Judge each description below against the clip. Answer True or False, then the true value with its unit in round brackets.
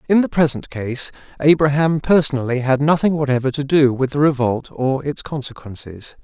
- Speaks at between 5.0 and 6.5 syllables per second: True (5.2 syllables/s)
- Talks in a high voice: False (140 Hz)